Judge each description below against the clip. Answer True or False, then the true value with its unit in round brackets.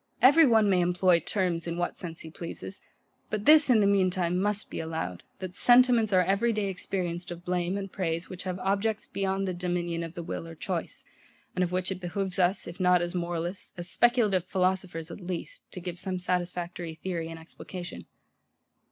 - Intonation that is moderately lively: False (2.2 semitones)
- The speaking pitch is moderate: True (180 Hz)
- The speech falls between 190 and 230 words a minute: True (195 wpm)